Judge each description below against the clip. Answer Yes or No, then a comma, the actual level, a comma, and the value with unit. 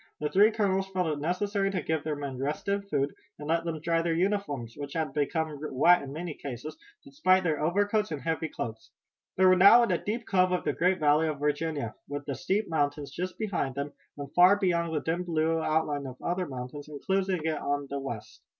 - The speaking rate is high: Yes, fast, 215 wpm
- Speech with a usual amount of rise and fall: Yes, average, 4.3 semitones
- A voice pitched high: No, medium, 160 Hz